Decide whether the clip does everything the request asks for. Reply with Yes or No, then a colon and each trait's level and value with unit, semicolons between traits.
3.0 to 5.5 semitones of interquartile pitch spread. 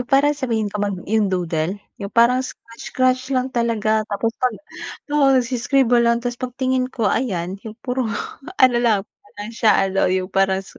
Yes: average, 3.9 semitones